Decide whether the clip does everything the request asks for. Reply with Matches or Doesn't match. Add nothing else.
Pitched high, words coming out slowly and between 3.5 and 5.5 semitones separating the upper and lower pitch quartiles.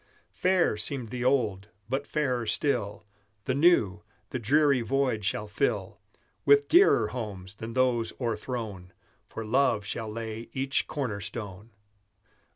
Doesn't match